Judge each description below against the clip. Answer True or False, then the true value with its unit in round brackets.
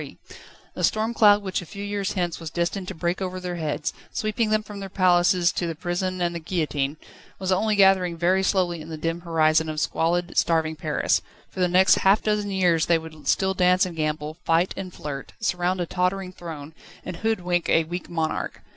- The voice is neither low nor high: True (175 Hz)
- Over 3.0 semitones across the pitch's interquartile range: False (2.7 semitones)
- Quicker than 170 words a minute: True (200 wpm)